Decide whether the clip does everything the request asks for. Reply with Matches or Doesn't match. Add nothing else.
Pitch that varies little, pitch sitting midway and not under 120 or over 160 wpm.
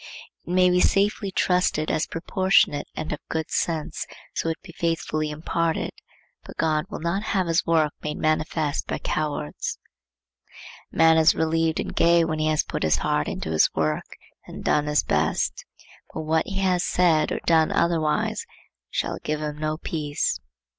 Doesn't match